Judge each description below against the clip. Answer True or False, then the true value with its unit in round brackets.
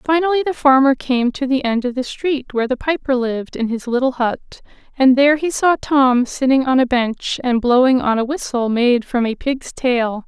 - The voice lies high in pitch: True (260 Hz)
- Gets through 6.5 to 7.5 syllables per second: False (5.1 syllables/s)